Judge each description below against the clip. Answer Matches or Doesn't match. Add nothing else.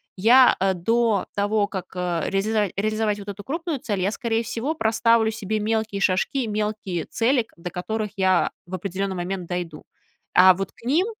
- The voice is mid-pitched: Doesn't match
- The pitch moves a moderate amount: Matches